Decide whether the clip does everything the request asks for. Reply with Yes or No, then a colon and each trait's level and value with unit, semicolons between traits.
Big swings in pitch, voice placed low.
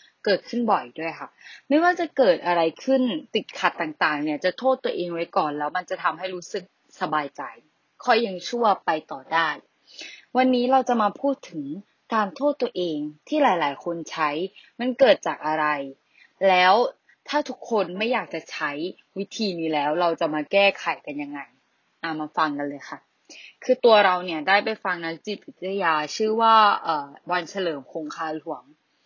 No: wide, 6.8 semitones; medium, 185 Hz